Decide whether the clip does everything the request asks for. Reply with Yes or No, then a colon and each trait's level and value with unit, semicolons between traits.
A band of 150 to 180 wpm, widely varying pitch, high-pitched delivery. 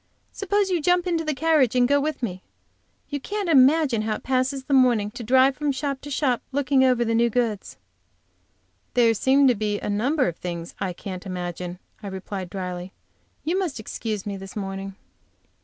No: average, 190 wpm; wide, 6.1 semitones; high, 245 Hz